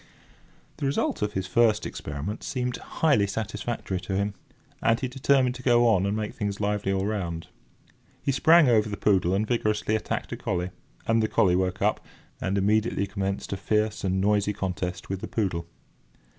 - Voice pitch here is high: No, low, 105 Hz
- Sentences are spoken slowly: No, average, 180 wpm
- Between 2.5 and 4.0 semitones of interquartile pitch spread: Yes, average, 2.9 semitones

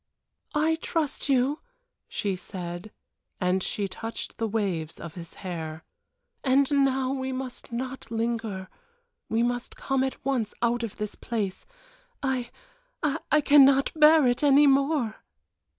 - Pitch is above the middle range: Yes, high, 245 Hz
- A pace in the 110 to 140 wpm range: Yes, slow, 135 wpm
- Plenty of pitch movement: No, average, 4.9 semitones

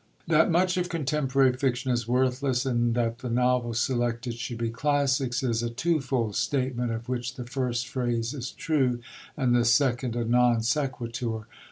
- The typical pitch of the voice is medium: No, low, 125 Hz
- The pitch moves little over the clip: Yes, narrow, 2.1 semitones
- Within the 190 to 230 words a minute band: No, average, 165 wpm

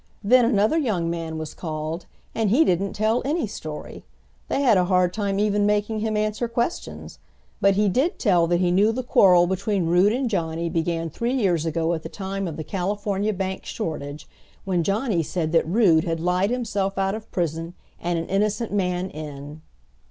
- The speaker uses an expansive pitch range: No, average, 4.1 semitones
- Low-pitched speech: No, high, 190 Hz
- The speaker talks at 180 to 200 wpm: Yes, average, 190 wpm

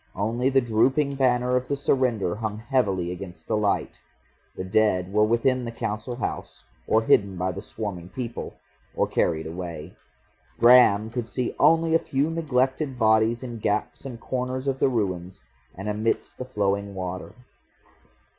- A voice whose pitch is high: No, low, 115 Hz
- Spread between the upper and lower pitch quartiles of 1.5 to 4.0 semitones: No, average, 4.4 semitones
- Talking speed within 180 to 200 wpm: No, average, 155 wpm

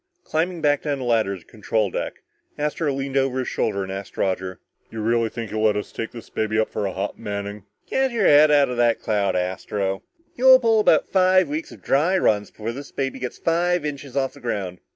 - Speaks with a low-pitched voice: Yes, low, 120 Hz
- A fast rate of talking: Yes, fast, 230 wpm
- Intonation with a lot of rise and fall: Yes, wide, 6.4 semitones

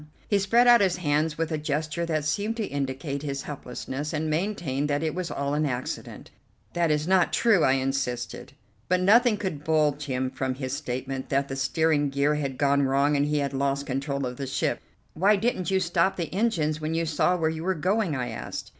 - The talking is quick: Yes, fast, 210 wpm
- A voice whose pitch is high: No, medium, 150 Hz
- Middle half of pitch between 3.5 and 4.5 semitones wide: Yes, average, 4.0 semitones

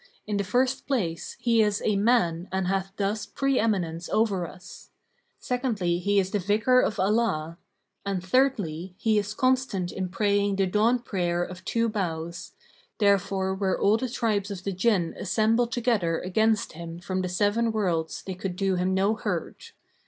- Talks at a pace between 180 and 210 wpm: No, average, 170 wpm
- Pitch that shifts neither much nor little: Yes, average, 3.5 semitones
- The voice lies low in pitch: No, high, 200 Hz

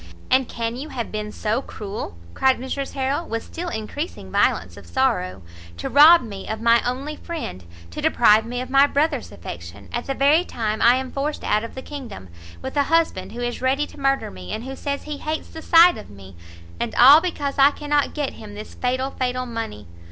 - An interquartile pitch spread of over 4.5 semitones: Yes, average, 5.0 semitones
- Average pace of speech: No, fast, 210 wpm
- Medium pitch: No, very high, 255 Hz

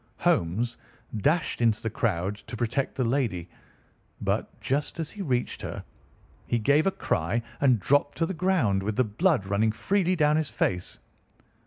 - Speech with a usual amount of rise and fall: No, wide, 6.6 semitones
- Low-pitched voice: Yes, low, 120 Hz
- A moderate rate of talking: Yes, average, 165 wpm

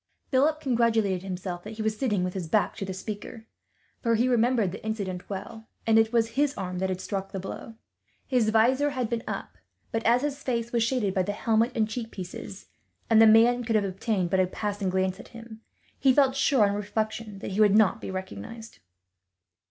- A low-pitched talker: No, high, 220 Hz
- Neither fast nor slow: No, fast, 210 wpm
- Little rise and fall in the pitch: No, average, 3.4 semitones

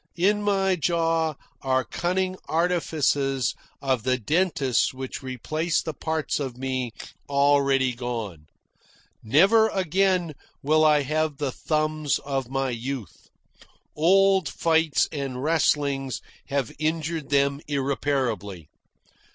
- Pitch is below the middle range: No, medium, 145 Hz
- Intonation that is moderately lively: Yes, average, 3.7 semitones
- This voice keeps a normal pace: No, slow, 110 wpm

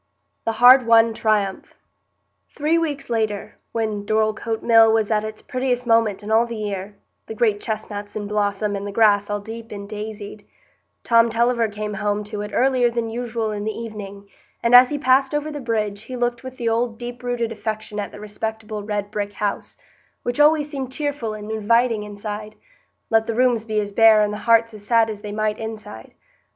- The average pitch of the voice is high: Yes, high, 220 Hz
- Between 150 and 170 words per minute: No, average, 190 wpm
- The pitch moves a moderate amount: No, narrow, 2.1 semitones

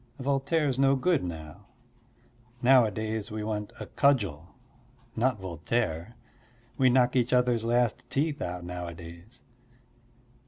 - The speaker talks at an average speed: No, slow, 110 wpm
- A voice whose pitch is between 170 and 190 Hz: No, low, 115 Hz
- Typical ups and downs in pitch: No, wide, 6.5 semitones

